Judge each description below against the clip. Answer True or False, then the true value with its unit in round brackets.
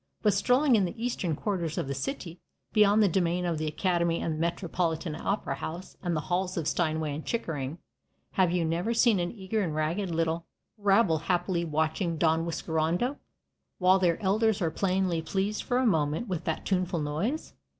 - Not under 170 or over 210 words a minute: True (180 wpm)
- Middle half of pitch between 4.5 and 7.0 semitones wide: False (3.6 semitones)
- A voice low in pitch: False (175 Hz)